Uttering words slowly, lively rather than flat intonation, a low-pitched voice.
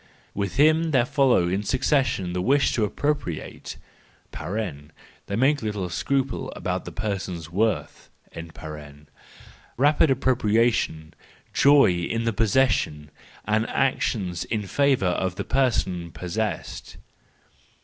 Yes: slow, 110 wpm; wide, 6.7 semitones; low, 110 Hz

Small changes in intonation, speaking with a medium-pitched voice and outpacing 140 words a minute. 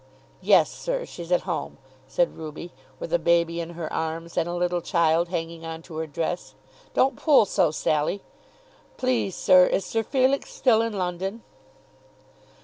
No: average, 3.2 semitones; medium, 175 Hz; average, 160 wpm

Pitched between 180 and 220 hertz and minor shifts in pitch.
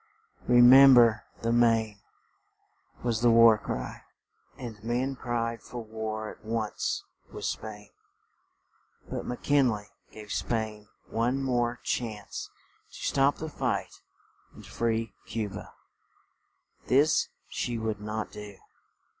No: low, 115 Hz; narrow, 2.0 semitones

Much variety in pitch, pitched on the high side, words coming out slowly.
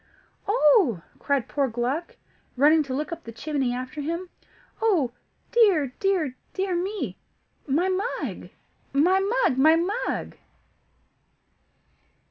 Yes: wide, 5.9 semitones; very high, 315 Hz; slow, 110 wpm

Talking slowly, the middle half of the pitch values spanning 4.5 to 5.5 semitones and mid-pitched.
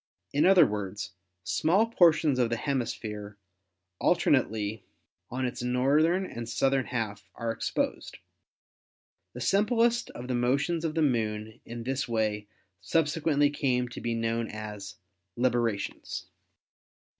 No: slow, 125 wpm; average, 5.1 semitones; low, 125 Hz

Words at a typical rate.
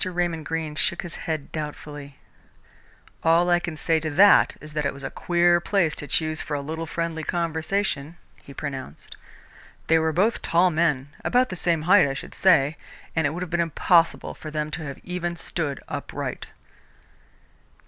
Yes: average, 180 wpm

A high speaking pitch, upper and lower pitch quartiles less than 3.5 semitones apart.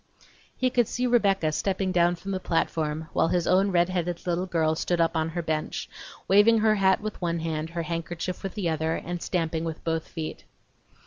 No: medium, 175 Hz; average, 2.8 semitones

